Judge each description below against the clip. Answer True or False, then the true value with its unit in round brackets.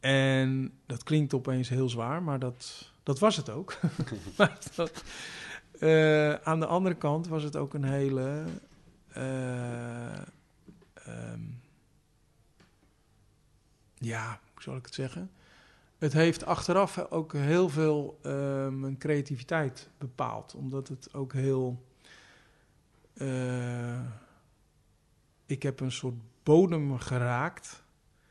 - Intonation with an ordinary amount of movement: True (3.4 semitones)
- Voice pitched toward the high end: False (135 Hz)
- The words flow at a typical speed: False (110 wpm)